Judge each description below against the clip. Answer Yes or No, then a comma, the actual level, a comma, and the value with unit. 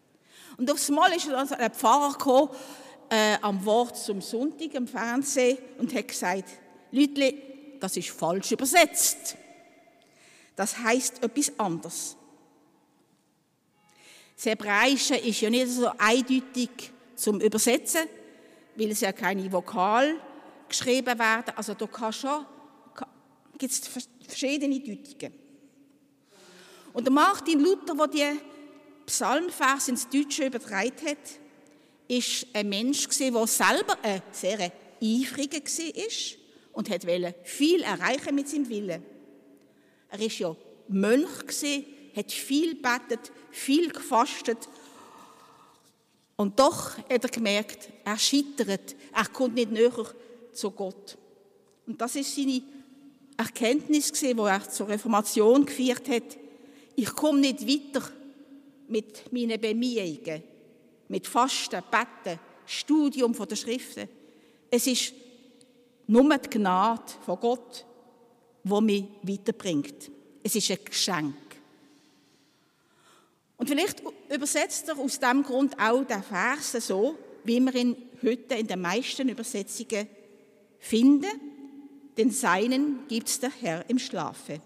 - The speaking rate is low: Yes, slow, 120 wpm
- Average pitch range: Yes, average, 4.3 semitones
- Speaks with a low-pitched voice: No, high, 245 Hz